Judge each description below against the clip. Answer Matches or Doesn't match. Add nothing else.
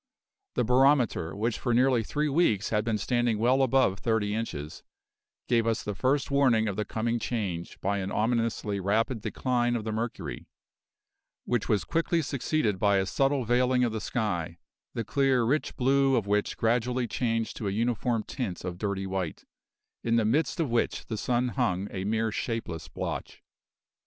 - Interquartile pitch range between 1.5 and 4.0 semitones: Matches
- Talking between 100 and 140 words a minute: Doesn't match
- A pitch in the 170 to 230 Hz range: Doesn't match